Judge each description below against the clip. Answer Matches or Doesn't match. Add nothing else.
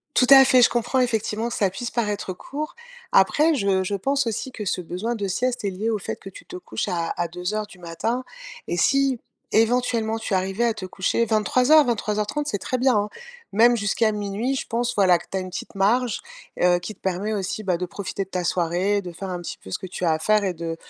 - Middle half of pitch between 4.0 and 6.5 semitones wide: Matches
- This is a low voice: Doesn't match